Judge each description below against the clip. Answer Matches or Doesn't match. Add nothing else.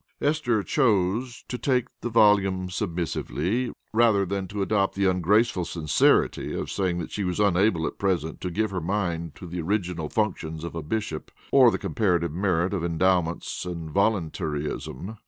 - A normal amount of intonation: Matches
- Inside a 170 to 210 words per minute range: Doesn't match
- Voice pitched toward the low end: Matches